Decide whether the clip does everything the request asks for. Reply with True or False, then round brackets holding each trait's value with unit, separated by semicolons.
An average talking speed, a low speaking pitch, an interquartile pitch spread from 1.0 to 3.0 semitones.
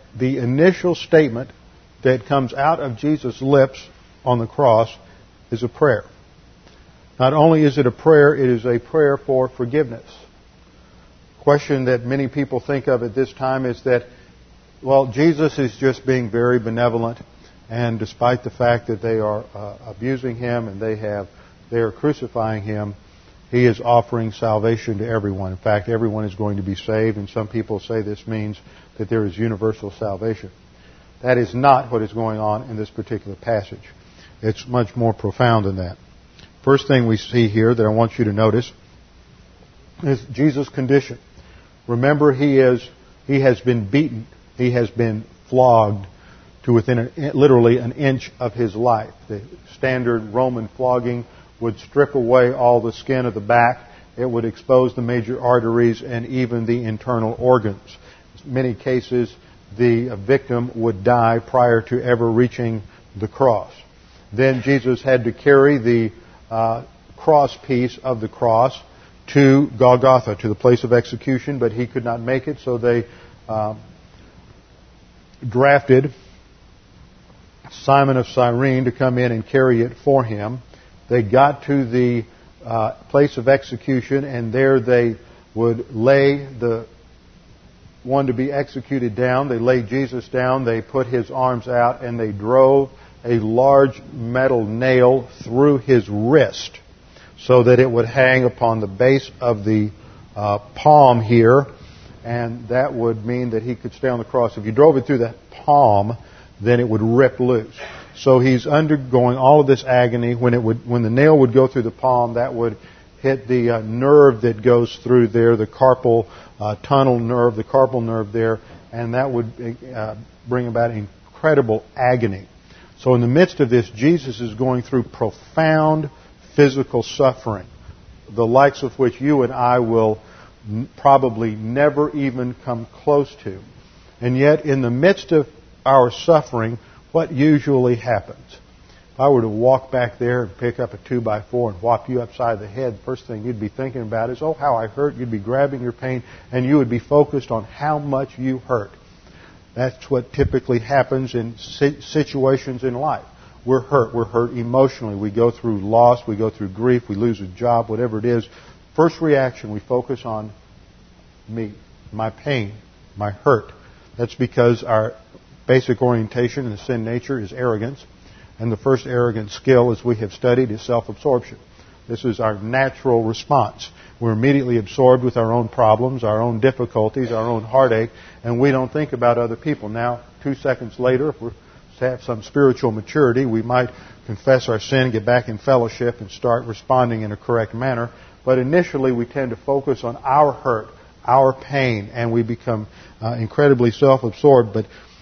True (170 wpm; 120 Hz; 2.7 semitones)